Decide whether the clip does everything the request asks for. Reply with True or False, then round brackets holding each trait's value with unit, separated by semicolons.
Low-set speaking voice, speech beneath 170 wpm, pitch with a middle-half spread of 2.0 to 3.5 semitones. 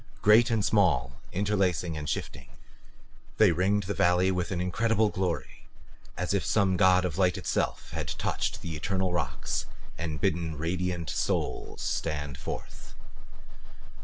True (90 Hz; 135 wpm; 3.0 semitones)